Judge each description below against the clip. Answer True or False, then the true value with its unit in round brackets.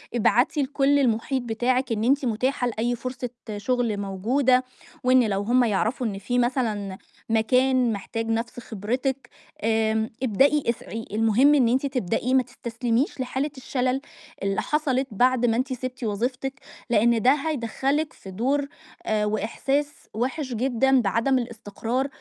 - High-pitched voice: True (245 Hz)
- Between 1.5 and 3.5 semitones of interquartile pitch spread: True (2.9 semitones)